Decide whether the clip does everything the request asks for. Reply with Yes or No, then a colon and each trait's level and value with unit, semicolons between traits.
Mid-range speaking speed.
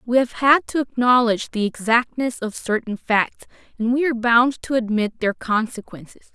Yes: average, 170 wpm